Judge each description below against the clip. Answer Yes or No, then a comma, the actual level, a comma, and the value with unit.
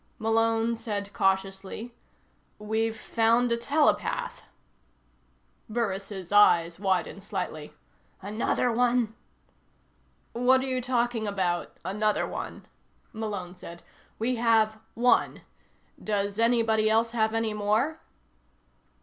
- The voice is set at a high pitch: Yes, high, 220 Hz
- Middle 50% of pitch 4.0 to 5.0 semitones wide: No, average, 2.7 semitones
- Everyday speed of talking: No, slow, 100 wpm